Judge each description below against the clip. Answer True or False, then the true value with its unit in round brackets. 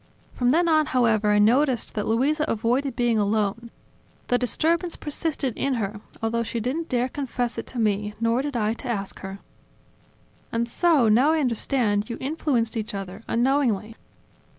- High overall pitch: True (235 Hz)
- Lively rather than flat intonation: False (4.1 semitones)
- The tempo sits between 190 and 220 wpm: False (165 wpm)